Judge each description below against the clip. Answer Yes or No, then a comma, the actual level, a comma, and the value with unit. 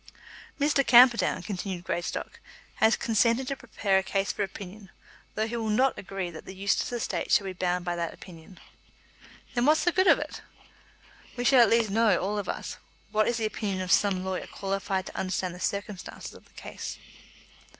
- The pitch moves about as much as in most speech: Yes, average, 3.7 semitones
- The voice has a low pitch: No, high, 200 Hz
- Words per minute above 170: Yes, average, 190 wpm